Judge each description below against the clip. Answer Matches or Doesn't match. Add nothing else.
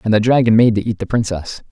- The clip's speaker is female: Doesn't match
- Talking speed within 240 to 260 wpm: Doesn't match